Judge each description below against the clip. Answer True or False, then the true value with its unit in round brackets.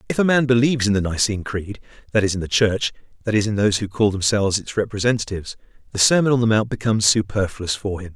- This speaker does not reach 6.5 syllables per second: False (6.9 syllables/s)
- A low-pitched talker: True (105 Hz)